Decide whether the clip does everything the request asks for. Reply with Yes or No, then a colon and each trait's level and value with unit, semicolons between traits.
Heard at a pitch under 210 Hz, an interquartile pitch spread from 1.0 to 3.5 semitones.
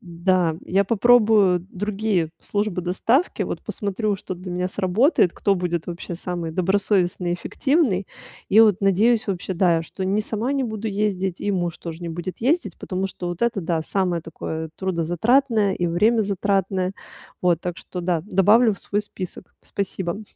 Yes: high, 190 Hz; average, 3.2 semitones